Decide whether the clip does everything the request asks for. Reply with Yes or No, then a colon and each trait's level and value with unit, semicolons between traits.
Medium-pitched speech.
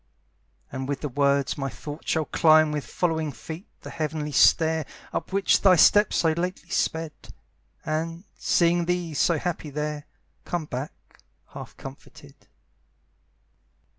Yes: medium, 155 Hz